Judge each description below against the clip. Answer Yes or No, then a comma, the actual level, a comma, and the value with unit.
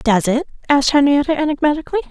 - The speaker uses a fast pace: No, average, 140 wpm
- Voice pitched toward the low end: No, very high, 290 Hz